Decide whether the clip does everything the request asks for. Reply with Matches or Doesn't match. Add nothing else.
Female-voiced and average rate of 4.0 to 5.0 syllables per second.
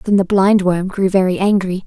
Matches